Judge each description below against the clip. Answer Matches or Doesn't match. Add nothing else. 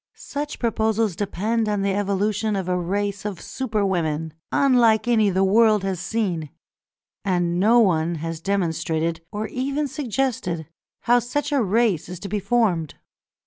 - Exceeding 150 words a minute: Doesn't match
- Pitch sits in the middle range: Doesn't match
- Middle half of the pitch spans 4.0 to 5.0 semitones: Matches